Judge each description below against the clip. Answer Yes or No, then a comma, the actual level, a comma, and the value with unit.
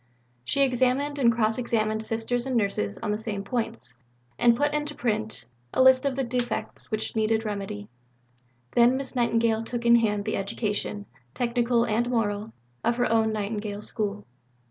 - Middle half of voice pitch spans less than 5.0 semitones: Yes, narrow, 2.4 semitones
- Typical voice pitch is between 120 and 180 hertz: No, high, 230 Hz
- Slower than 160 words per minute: No, average, 165 wpm